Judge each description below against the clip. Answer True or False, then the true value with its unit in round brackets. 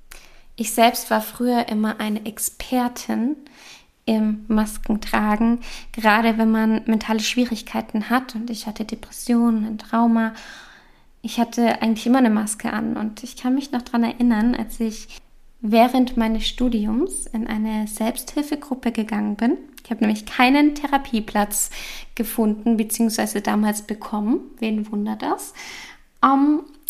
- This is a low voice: False (230 Hz)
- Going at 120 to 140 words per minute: True (130 wpm)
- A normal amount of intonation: False (2.3 semitones)